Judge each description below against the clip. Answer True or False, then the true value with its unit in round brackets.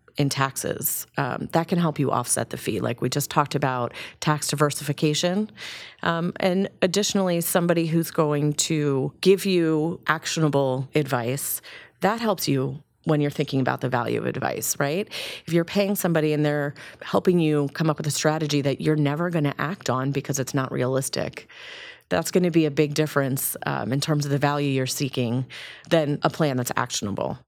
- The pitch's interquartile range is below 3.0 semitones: False (3.3 semitones)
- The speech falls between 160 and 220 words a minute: True (185 wpm)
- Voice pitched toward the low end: False (150 Hz)